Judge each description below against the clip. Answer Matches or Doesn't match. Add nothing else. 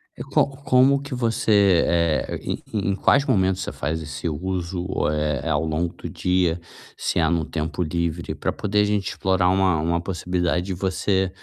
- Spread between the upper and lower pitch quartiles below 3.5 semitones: Matches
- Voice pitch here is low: Matches